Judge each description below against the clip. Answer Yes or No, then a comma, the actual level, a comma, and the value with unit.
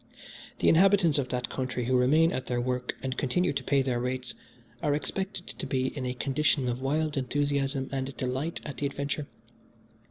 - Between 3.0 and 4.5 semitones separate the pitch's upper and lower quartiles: No, narrow, 2.5 semitones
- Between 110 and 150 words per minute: No, average, 185 wpm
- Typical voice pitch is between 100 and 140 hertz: Yes, low, 135 Hz